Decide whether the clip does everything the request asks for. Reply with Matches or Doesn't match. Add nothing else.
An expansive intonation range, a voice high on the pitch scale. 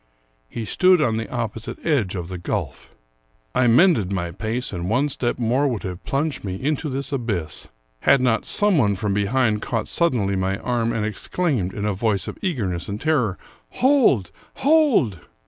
Doesn't match